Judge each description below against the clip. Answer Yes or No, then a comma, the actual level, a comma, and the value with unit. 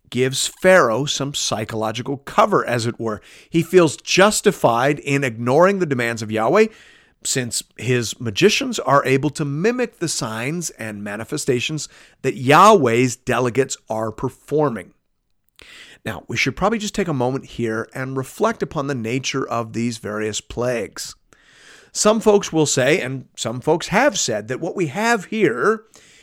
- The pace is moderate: Yes, average, 150 wpm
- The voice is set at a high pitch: No, low, 135 Hz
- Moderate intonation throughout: No, wide, 6.8 semitones